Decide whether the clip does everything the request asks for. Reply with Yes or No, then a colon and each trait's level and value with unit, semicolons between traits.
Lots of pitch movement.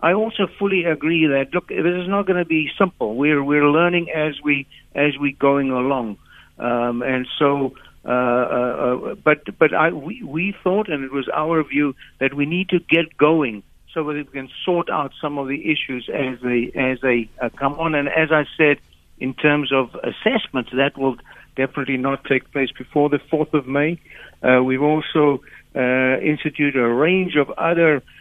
No: average, 3.2 semitones